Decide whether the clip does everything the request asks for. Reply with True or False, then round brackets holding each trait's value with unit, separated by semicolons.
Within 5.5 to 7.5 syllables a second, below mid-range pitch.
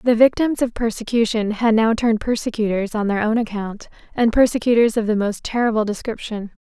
False (5.7 syllables/s; 225 Hz)